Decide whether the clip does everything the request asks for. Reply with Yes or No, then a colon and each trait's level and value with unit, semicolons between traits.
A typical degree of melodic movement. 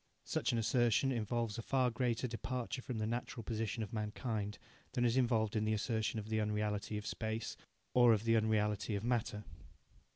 No: narrow, 2.0 semitones